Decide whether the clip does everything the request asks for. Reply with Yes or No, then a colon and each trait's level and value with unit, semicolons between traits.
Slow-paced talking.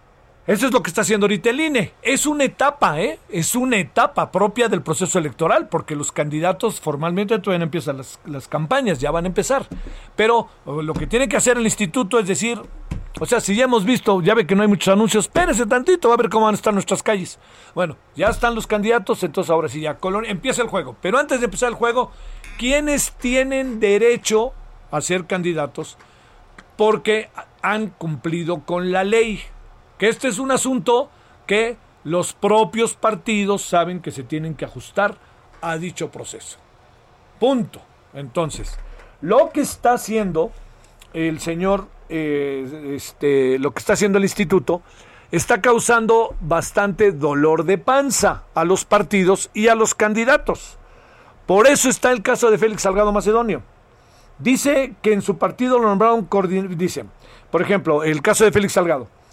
No: average, 170 wpm